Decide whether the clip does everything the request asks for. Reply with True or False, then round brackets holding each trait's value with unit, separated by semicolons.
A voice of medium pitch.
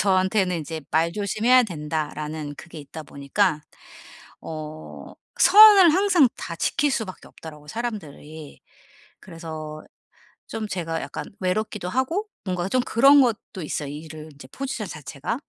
True (175 Hz)